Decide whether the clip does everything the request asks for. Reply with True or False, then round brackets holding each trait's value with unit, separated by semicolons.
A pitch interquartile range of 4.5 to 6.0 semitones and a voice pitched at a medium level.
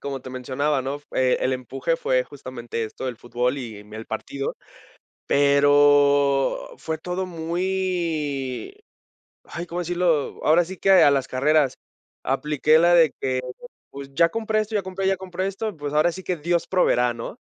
True (5.0 semitones; 145 Hz)